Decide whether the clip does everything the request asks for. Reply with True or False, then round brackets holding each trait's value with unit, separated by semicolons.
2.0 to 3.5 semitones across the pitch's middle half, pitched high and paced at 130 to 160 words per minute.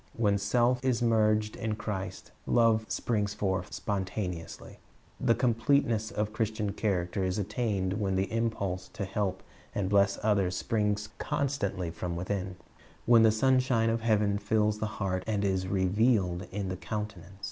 False (2.8 semitones; 105 Hz; 150 wpm)